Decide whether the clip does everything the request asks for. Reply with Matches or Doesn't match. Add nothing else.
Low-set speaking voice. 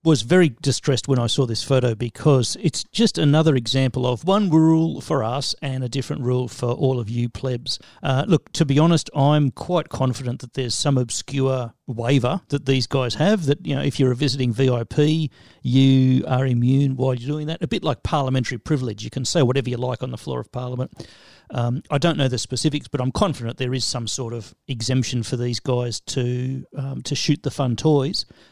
Matches